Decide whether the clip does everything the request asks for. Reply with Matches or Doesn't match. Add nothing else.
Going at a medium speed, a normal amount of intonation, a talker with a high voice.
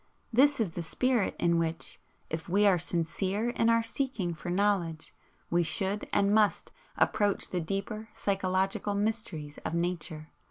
Matches